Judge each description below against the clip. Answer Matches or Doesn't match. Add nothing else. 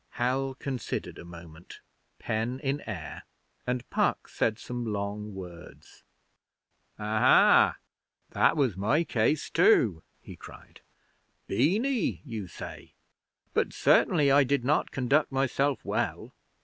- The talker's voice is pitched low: Matches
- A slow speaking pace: Matches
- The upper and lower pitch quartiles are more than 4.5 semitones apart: Matches